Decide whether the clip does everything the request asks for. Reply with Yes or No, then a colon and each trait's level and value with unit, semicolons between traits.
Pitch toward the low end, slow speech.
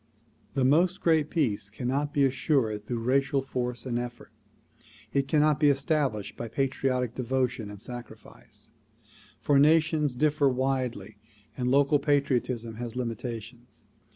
Yes: low, 130 Hz; slow, 125 wpm